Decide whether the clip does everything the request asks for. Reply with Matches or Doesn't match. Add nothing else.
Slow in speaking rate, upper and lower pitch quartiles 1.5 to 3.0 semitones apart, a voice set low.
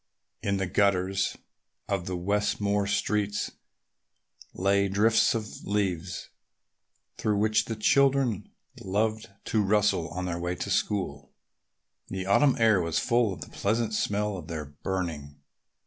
Matches